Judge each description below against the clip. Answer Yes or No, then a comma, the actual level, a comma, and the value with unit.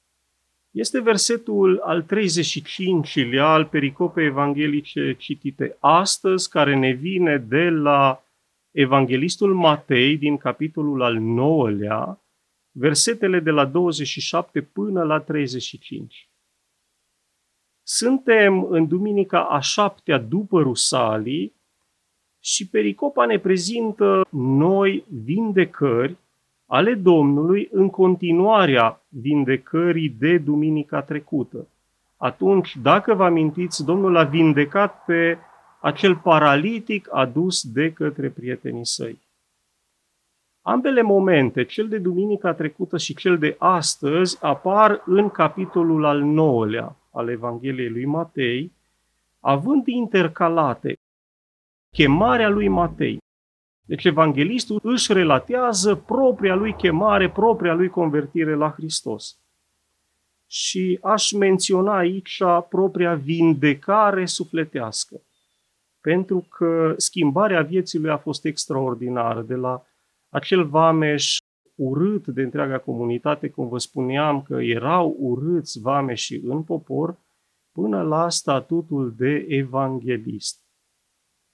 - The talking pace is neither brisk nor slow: No, slow, 100 wpm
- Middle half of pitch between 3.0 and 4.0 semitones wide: No, average, 5.2 semitones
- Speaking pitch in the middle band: Yes, medium, 155 Hz